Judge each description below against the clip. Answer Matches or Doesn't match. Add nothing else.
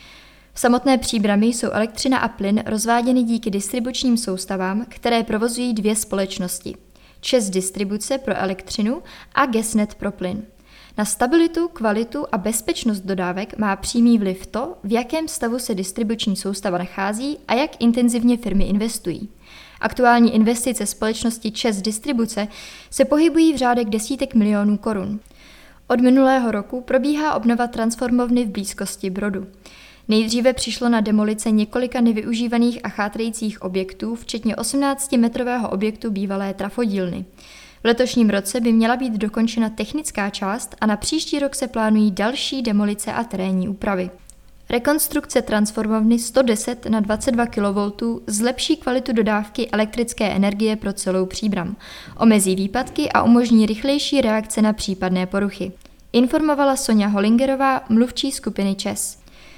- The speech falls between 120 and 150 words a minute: Matches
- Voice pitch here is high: Matches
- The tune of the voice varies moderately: Matches